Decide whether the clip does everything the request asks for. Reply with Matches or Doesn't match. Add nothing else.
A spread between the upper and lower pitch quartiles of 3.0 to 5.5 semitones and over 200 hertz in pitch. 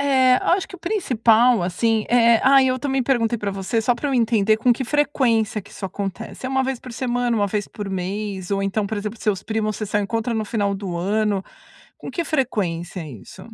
Matches